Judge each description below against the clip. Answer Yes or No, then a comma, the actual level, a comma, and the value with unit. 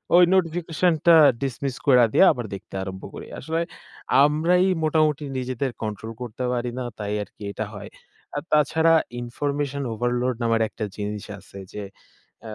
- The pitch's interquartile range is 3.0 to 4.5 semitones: No, wide, 5.4 semitones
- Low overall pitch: Yes, low, 130 Hz